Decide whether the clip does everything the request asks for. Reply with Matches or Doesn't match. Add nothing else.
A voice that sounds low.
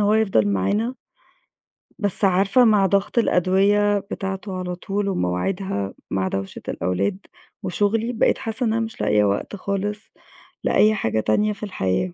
Doesn't match